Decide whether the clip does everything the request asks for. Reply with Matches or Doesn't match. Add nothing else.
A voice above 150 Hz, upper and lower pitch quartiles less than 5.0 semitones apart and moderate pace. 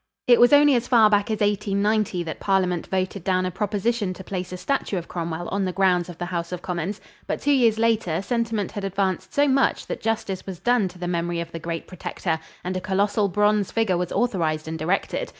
Doesn't match